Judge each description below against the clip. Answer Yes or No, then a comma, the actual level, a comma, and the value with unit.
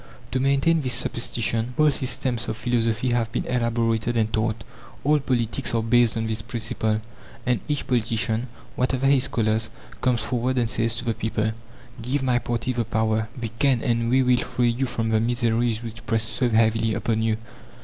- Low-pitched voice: Yes, low, 115 Hz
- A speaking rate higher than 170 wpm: Yes, average, 180 wpm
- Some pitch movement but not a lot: No, narrow, 2.0 semitones